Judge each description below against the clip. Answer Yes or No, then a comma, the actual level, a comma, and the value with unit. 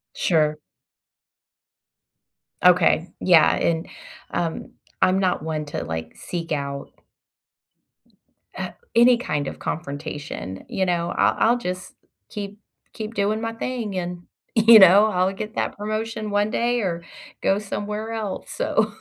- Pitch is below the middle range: No, high, 190 Hz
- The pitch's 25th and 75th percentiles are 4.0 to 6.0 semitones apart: Yes, average, 4.4 semitones